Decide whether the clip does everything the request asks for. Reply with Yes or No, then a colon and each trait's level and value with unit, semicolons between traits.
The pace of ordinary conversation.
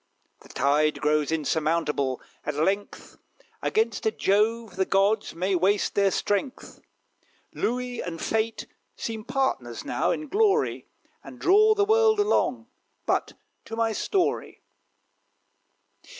No: slow, 120 wpm